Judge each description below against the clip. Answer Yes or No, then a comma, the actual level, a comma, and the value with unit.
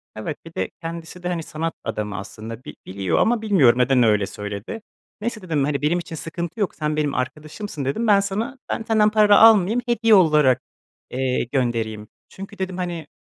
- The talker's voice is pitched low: No, medium, 160 Hz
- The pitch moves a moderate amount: No, wide, 8.0 semitones